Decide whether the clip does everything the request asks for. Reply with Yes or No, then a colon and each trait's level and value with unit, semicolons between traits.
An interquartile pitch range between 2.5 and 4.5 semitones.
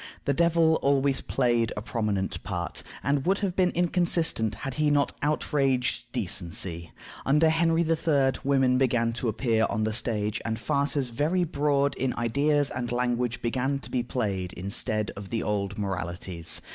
No: average, 5.0 semitones